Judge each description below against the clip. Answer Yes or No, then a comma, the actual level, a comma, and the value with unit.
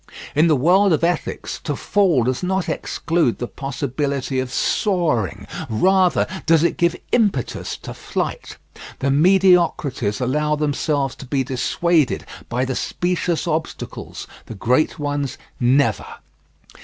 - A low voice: No, medium, 150 Hz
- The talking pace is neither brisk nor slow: No, slow, 130 wpm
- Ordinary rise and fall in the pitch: Yes, average, 5.0 semitones